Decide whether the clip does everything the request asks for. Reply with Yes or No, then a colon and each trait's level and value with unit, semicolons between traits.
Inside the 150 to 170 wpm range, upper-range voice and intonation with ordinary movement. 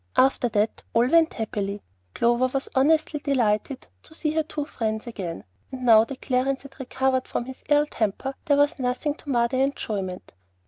No: average, 180 wpm; very high, 260 Hz; average, 3.9 semitones